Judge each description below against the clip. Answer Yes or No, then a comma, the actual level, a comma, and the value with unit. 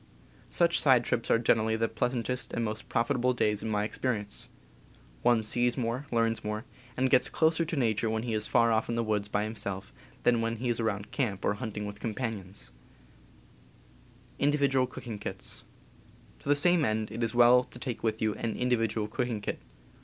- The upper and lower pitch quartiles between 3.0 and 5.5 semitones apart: No, narrow, 2.5 semitones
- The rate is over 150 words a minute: Yes, average, 180 wpm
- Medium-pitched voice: No, low, 115 Hz